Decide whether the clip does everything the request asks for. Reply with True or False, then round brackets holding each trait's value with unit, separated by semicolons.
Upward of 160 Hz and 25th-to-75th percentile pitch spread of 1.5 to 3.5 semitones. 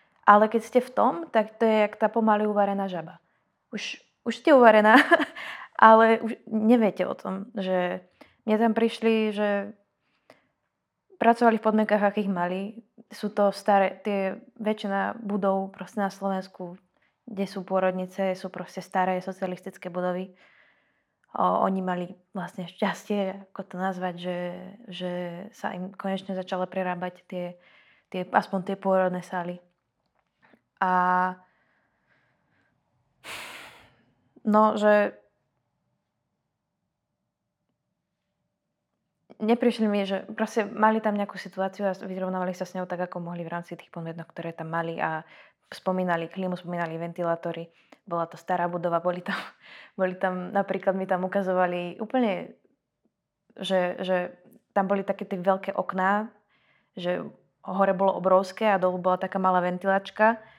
True (190 Hz; 2.6 semitones)